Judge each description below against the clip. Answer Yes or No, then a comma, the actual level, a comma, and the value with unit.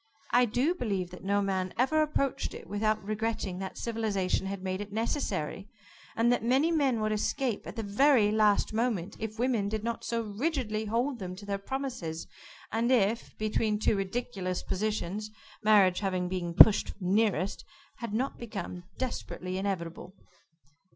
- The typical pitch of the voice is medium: No, high, 215 Hz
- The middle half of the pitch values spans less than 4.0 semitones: Yes, average, 3.4 semitones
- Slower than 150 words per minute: No, average, 160 wpm